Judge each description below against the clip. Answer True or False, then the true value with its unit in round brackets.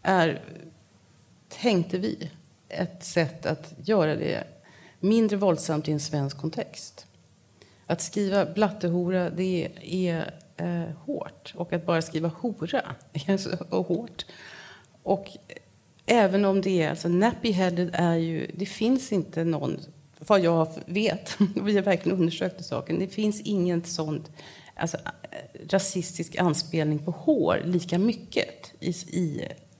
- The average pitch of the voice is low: False (175 Hz)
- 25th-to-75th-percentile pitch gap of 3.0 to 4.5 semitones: True (3.4 semitones)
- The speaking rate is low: True (125 wpm)